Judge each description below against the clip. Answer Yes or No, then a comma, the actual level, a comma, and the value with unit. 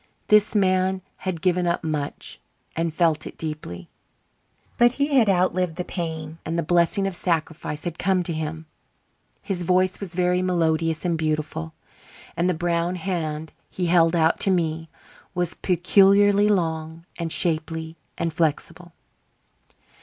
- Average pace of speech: Yes, average, 145 wpm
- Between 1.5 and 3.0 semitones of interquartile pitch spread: Yes, narrow, 2.4 semitones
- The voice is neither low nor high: Yes, medium, 170 Hz